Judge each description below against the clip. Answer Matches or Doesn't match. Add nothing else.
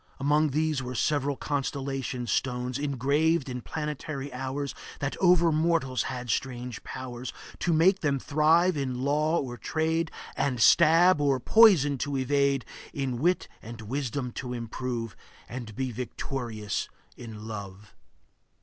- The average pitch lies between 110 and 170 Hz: Matches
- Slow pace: Matches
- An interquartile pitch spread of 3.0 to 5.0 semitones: Matches